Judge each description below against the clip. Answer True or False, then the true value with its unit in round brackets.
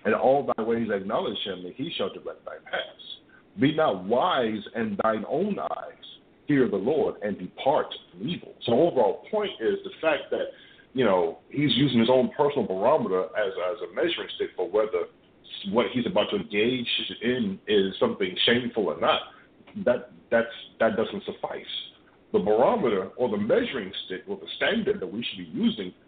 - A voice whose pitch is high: True (230 Hz)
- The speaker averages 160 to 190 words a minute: True (180 wpm)